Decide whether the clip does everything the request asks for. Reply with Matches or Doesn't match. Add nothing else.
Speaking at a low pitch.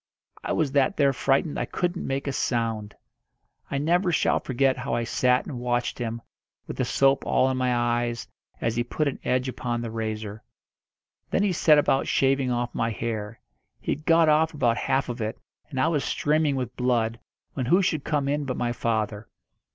Matches